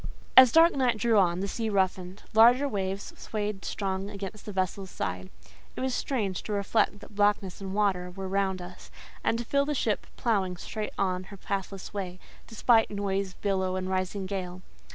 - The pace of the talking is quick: No, average, 180 wpm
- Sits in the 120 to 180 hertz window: No, high, 200 Hz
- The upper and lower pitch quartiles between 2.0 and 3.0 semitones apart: Yes, narrow, 2.4 semitones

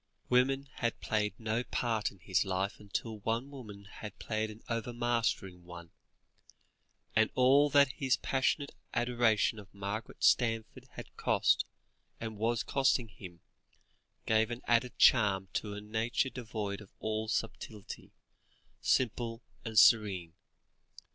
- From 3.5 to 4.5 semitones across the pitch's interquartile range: No, average, 2.7 semitones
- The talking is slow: Yes, slow, 130 wpm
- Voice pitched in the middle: No, low, 110 Hz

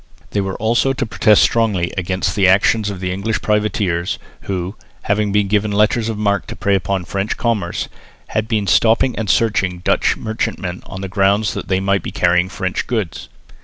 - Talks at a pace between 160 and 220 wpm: Yes, average, 180 wpm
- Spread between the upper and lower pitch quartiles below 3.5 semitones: Yes, narrow, 2.6 semitones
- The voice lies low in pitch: Yes, low, 100 Hz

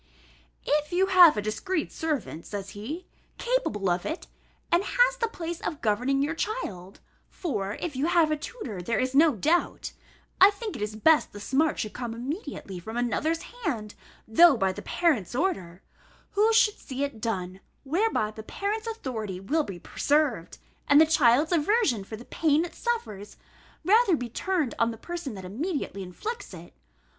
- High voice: Yes, very high, 285 Hz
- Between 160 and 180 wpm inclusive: Yes, average, 170 wpm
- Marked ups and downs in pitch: Yes, wide, 8.4 semitones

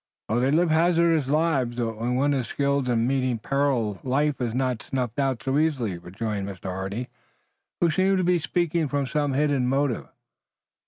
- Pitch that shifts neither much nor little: Yes, average, 4.1 semitones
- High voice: No, low, 135 Hz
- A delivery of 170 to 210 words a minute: Yes, average, 175 wpm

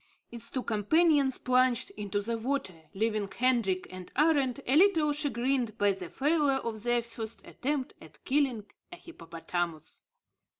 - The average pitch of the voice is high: Yes, high, 240 Hz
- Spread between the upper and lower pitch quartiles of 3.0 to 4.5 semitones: No, average, 5.3 semitones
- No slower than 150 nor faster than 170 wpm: No, average, 140 wpm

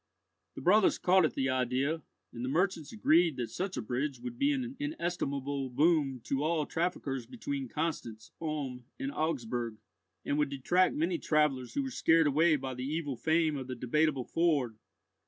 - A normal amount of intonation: Yes, average, 4.8 semitones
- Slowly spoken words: No, average, 175 wpm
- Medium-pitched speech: Yes, medium, 150 Hz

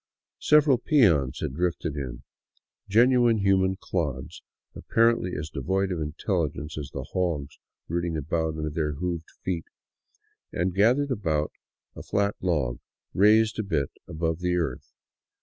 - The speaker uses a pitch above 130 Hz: No, very low, 85 Hz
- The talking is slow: Yes, slow, 130 wpm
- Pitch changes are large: No, average, 4.6 semitones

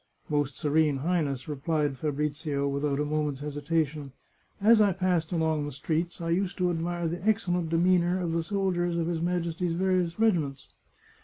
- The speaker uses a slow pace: No, average, 175 wpm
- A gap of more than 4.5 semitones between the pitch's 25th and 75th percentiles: No, average, 3.1 semitones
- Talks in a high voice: No, medium, 165 Hz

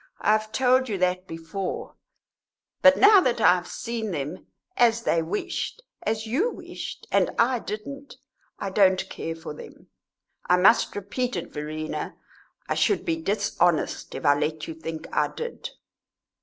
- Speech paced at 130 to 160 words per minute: Yes, average, 155 wpm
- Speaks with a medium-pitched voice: No, high, 200 Hz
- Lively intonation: Yes, wide, 6.6 semitones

